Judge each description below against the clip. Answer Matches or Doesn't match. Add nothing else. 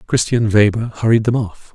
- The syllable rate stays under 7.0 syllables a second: Matches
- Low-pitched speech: Matches